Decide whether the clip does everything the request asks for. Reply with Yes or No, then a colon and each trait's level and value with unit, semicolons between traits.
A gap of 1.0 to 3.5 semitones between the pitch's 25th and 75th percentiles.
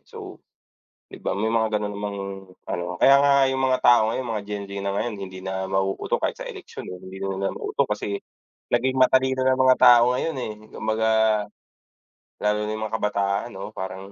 No: average, 3.9 semitones